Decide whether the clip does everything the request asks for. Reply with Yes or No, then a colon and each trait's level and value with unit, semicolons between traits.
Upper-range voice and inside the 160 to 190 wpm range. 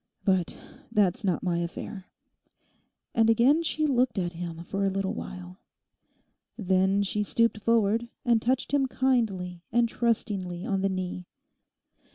No: high, 200 Hz; average, 140 wpm